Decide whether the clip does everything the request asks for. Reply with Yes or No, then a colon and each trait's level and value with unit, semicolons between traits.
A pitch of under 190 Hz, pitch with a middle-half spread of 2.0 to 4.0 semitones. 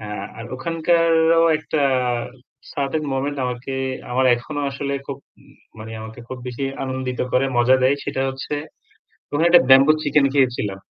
Yes: low, 135 Hz; average, 2.9 semitones